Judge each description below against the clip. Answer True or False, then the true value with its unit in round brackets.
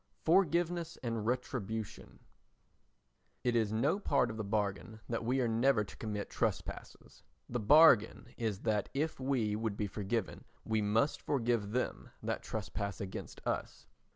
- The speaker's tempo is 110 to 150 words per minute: True (145 wpm)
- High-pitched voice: False (115 Hz)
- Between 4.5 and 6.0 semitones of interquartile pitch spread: False (3.8 semitones)